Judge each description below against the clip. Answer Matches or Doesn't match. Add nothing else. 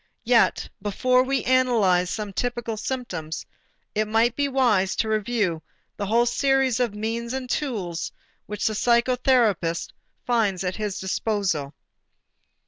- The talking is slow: Matches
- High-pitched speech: Matches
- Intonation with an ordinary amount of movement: Matches